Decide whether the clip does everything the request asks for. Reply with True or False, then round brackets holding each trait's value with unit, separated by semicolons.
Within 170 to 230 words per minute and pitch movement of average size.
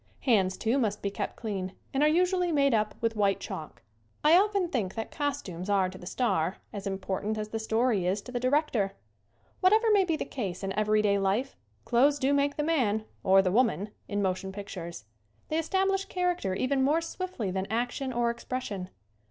False (190 wpm; 6.7 semitones)